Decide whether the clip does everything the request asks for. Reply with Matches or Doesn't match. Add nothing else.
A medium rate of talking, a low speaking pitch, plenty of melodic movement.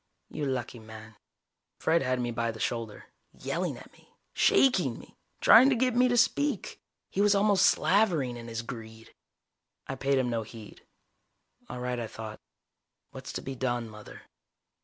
Matches